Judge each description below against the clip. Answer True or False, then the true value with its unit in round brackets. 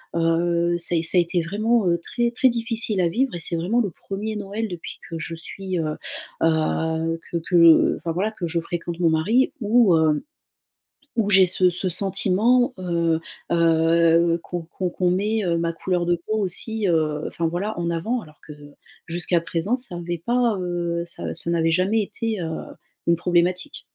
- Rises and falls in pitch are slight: False (3.7 semitones)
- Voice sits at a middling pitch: True (175 Hz)